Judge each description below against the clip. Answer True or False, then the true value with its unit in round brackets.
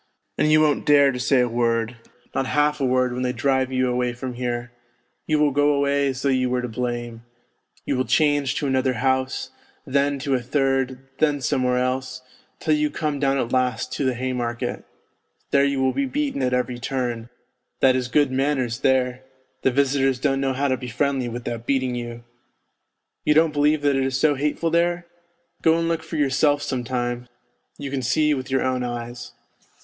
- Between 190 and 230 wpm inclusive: True (195 wpm)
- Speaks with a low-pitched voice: True (130 Hz)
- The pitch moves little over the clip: True (2.3 semitones)